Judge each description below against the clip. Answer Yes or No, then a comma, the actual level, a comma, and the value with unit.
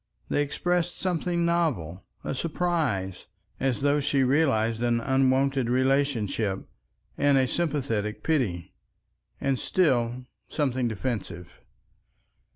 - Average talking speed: No, slow, 90 wpm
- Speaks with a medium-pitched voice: No, low, 130 Hz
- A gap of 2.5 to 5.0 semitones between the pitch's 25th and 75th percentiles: Yes, average, 4.4 semitones